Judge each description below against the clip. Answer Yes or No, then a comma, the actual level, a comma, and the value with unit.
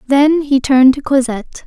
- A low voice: No, very high, 270 Hz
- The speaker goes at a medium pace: Yes, average, 180 wpm